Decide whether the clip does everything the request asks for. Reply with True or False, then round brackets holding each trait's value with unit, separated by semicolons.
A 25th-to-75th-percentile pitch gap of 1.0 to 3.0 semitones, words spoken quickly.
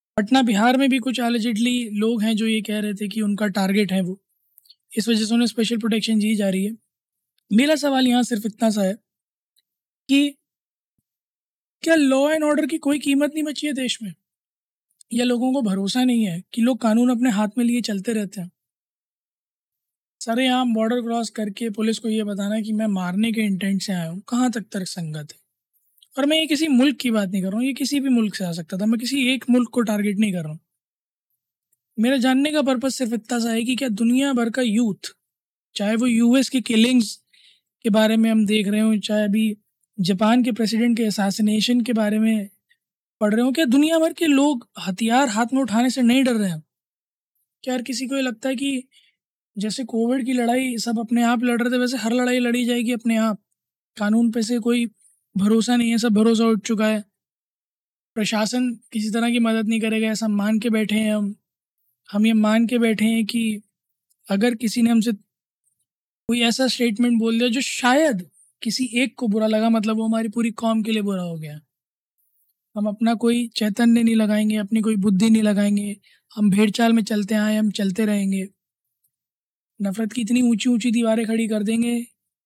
True (2.5 semitones; 205 wpm)